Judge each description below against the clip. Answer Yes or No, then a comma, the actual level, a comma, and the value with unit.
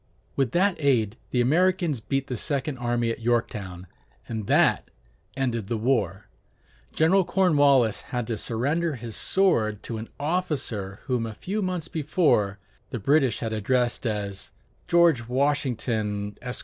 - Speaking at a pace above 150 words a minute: No, average, 140 wpm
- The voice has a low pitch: Yes, low, 125 Hz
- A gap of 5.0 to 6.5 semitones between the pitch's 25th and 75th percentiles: Yes, average, 5.3 semitones